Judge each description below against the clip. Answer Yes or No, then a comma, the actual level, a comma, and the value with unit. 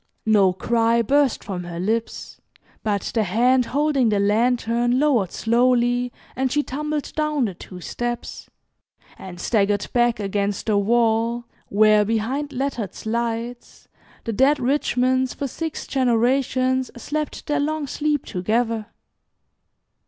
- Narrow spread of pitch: No, average, 3.5 semitones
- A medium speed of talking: No, slow, 125 wpm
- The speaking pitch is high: Yes, high, 240 Hz